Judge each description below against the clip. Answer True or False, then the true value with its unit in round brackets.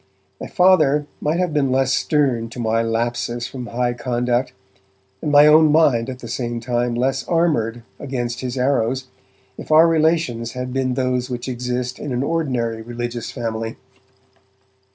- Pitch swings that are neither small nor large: True (3.1 semitones)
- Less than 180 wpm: True (155 wpm)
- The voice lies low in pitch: True (125 Hz)